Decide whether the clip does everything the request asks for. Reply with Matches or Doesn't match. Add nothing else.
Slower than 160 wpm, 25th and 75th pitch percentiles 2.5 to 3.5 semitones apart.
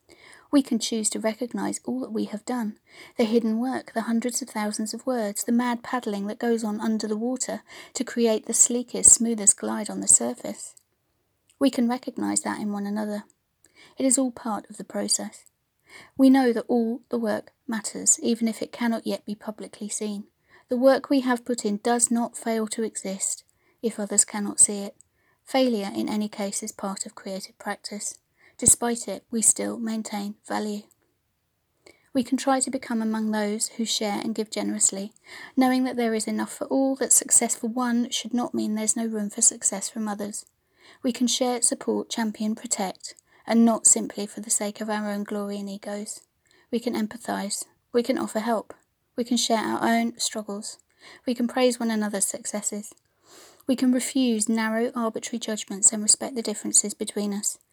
Doesn't match